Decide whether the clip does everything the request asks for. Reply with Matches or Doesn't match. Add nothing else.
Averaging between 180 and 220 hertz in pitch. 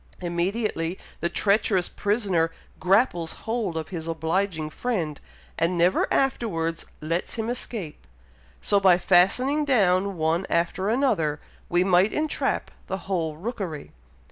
Matches